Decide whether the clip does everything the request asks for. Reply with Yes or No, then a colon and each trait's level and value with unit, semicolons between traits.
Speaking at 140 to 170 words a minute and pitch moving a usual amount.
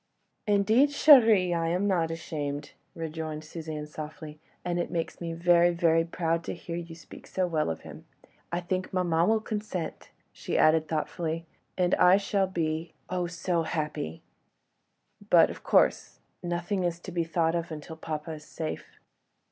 No: average, 155 wpm; narrow, 2.2 semitones